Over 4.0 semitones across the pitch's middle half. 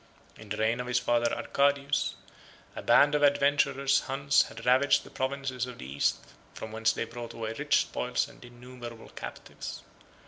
No: average, 3.0 semitones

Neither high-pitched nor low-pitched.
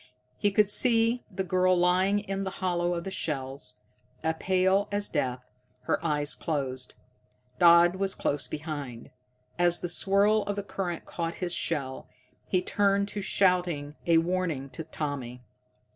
Yes: medium, 175 Hz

